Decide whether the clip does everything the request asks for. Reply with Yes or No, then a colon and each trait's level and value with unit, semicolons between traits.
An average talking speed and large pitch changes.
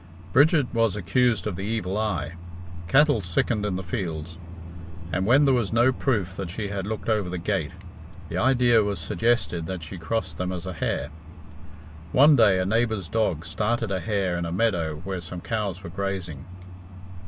No: average, 180 wpm; average, 4.4 semitones